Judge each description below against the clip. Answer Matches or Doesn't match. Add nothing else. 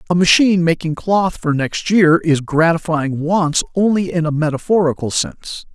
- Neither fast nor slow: Matches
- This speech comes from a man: Matches